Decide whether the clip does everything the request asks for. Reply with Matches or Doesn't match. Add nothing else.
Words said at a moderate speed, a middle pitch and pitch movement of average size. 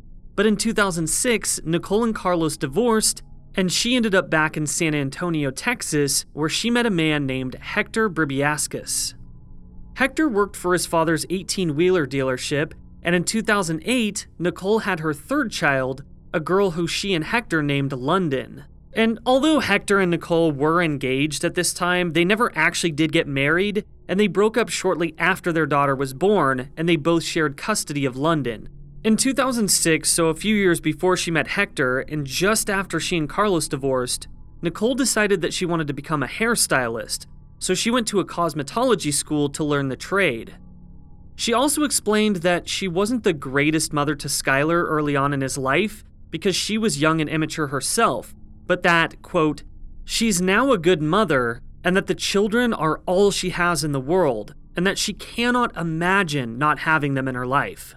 Matches